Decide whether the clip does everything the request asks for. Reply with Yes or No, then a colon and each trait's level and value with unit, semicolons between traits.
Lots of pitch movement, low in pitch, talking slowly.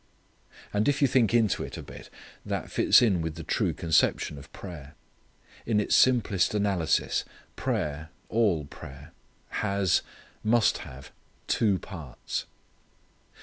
Yes: wide, 5.7 semitones; very low, 95 Hz; slow, 130 wpm